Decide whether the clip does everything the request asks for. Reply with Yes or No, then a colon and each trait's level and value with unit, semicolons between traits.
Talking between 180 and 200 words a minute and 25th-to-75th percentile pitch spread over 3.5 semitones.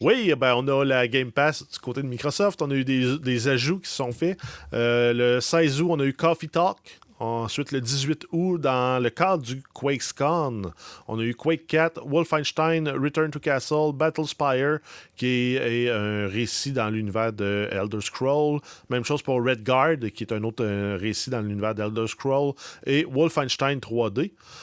Yes: average, 190 wpm; average, 4.3 semitones